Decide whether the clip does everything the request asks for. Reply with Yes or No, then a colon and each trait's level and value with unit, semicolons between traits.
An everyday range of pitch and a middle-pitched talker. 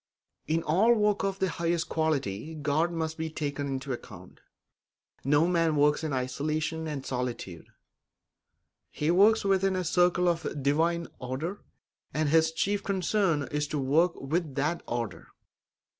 Yes: average, 3.4 semitones; medium, 160 Hz